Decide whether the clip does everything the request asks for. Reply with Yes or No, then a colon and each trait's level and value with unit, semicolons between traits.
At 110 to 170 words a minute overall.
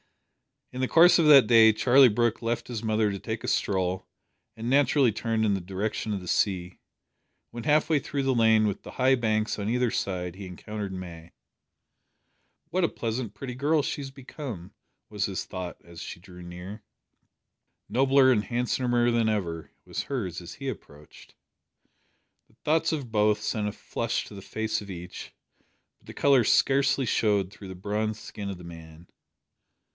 No: average, 180 wpm